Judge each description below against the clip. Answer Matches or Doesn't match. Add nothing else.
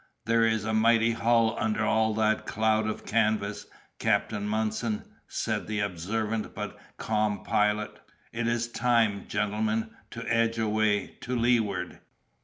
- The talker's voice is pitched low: Matches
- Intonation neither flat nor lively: Doesn't match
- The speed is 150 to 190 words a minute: Doesn't match